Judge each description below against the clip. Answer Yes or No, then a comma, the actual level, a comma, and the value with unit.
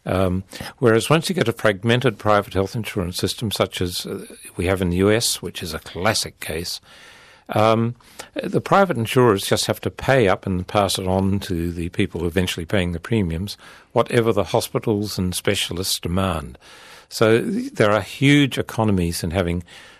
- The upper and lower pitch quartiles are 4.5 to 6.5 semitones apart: No, average, 3.8 semitones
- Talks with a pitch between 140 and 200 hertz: No, low, 100 Hz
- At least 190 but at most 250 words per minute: No, average, 170 wpm